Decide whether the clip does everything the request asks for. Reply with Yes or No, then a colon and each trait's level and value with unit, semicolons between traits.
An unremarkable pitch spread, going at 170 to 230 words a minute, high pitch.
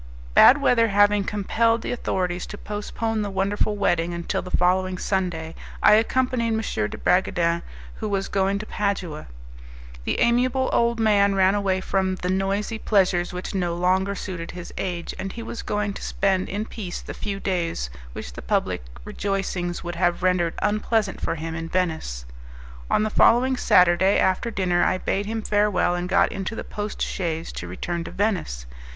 Yes: average, 3.0 semitones; average, 175 wpm; high, 195 Hz